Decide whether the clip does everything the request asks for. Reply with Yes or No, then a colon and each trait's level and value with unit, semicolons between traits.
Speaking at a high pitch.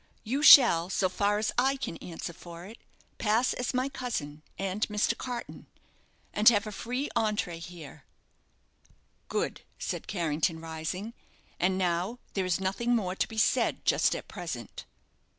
Yes: high, 200 Hz